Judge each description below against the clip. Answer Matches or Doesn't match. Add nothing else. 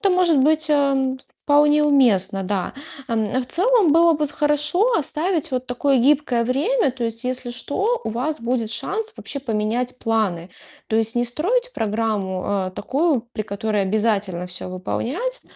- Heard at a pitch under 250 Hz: Doesn't match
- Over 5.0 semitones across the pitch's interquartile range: Matches